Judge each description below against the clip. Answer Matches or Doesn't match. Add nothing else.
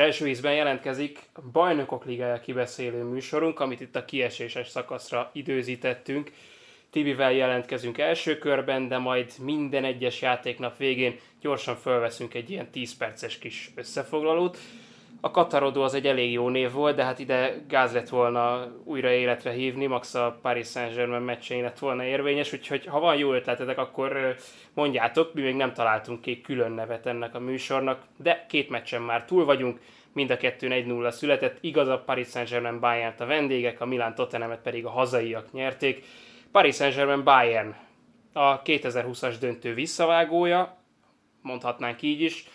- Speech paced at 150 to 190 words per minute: Matches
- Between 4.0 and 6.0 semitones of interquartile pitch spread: Doesn't match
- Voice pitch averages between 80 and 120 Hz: Doesn't match